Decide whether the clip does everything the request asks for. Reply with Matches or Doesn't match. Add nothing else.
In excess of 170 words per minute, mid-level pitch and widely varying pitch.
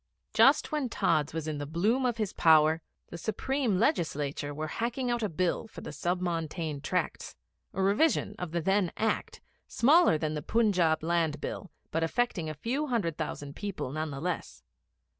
Matches